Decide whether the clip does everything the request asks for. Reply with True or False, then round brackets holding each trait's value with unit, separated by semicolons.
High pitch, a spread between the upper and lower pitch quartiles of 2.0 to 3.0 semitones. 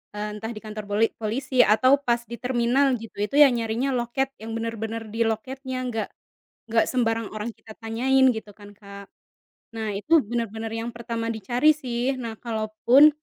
True (230 Hz; 2.7 semitones)